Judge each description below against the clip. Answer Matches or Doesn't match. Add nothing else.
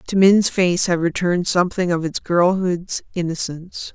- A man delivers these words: Doesn't match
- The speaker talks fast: Doesn't match